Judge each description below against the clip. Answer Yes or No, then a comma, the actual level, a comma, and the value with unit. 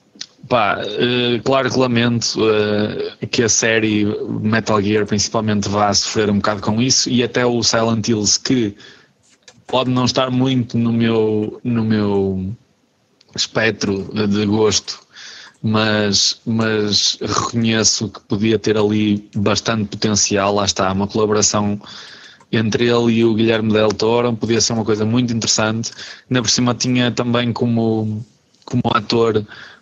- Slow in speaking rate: No, average, 140 wpm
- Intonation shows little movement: Yes, narrow, 2.0 semitones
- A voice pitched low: Yes, low, 110 Hz